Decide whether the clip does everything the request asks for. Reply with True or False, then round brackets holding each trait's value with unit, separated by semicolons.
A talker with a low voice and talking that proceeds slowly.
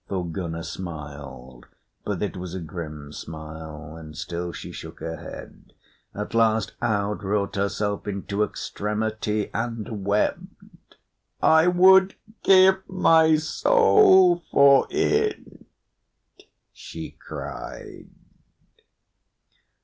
True (105 Hz; 95 wpm)